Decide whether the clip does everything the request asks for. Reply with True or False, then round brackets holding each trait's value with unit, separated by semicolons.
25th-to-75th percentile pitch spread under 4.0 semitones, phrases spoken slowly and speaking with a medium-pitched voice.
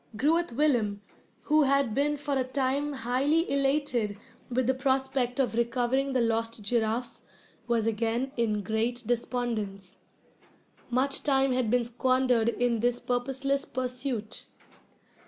False (2.7 semitones; 125 wpm; 250 Hz)